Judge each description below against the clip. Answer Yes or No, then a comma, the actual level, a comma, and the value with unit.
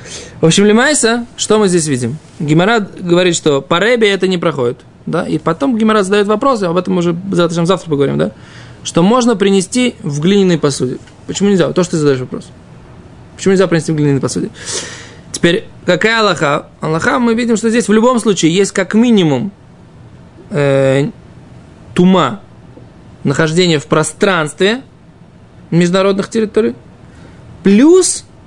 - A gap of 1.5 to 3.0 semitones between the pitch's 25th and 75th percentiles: No, average, 5.3 semitones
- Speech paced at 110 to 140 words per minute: No, average, 150 wpm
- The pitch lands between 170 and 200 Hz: Yes, medium, 185 Hz